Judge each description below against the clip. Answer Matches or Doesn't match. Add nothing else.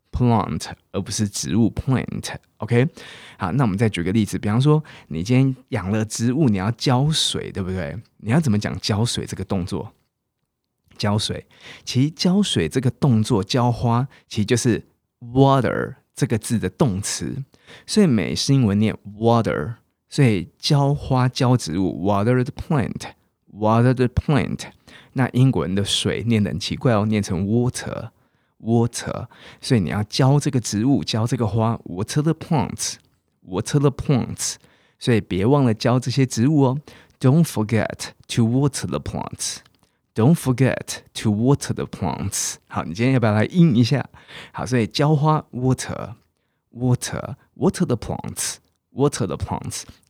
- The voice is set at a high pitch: Doesn't match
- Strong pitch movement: Doesn't match